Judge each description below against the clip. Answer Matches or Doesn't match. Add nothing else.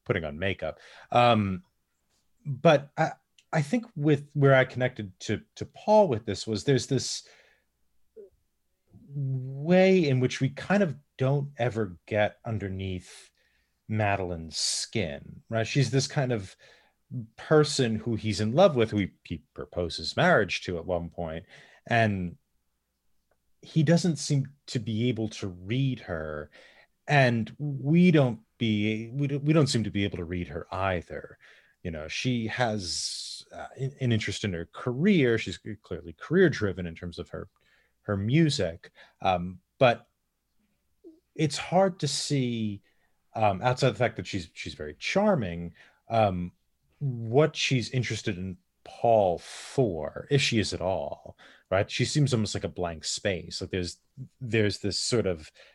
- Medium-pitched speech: Doesn't match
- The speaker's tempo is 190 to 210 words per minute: Doesn't match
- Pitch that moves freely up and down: Matches